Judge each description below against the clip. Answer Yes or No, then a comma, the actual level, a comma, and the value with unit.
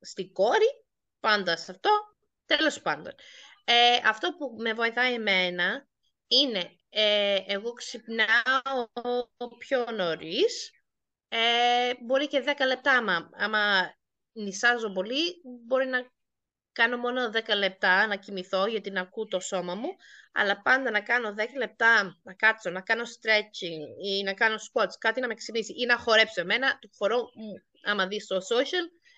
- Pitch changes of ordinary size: Yes, average, 3.7 semitones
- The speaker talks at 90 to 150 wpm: Yes, average, 145 wpm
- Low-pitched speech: No, high, 230 Hz